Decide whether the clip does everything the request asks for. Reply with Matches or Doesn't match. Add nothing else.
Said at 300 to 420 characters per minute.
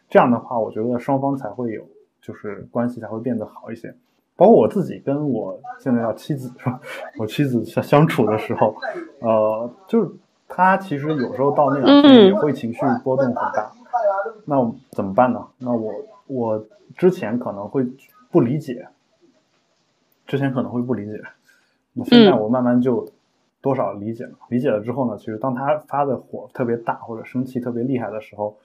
Doesn't match